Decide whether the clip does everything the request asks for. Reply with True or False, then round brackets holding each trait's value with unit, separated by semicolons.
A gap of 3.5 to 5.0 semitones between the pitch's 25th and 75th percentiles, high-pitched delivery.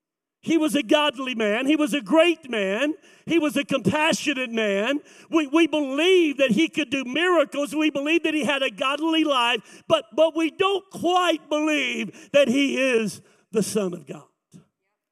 True (3.8 semitones; 295 Hz)